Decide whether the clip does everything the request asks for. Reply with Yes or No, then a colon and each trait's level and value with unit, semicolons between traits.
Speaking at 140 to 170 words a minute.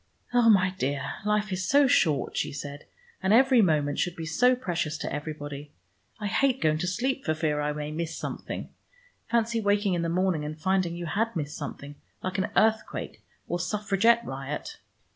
No: average, 180 wpm